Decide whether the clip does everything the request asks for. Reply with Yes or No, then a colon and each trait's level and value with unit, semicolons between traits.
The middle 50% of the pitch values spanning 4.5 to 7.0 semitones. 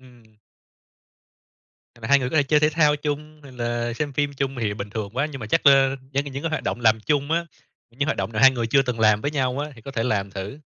No: average, 4.0 semitones